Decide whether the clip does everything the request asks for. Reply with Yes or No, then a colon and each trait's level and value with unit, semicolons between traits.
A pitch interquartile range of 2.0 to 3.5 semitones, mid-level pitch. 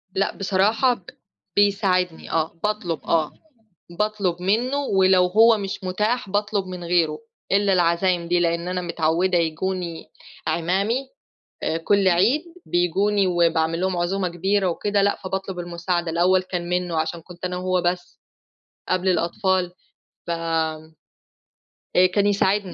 Yes: narrow, 2.5 semitones; medium, 180 Hz